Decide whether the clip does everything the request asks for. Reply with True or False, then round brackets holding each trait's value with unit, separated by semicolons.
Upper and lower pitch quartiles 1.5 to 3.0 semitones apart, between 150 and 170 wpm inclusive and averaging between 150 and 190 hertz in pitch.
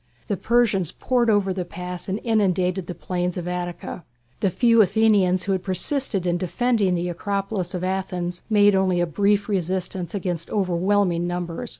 True (2.4 semitones; 165 wpm; 185 Hz)